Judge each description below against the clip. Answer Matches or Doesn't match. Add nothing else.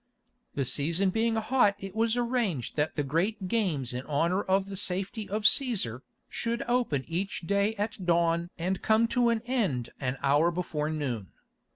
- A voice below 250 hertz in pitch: Matches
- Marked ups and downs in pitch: Matches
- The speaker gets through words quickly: Doesn't match